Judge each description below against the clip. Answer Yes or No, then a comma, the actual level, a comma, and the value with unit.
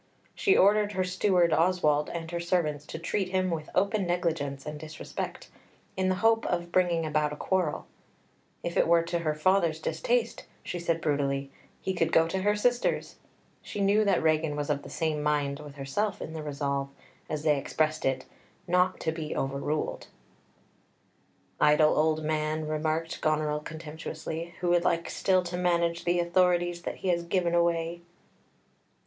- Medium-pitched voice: Yes, medium, 165 Hz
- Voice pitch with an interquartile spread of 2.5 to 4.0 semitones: Yes, average, 2.8 semitones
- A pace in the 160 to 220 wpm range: Yes, average, 165 wpm